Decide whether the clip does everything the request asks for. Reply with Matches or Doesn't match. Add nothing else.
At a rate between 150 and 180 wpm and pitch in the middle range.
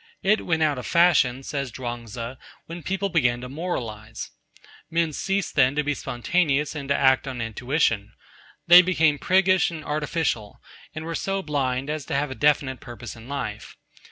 Matches